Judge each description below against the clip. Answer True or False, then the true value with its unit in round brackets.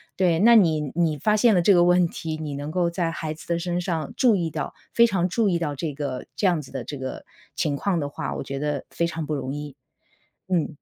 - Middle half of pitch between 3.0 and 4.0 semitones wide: True (3.3 semitones)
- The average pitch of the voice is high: False (165 Hz)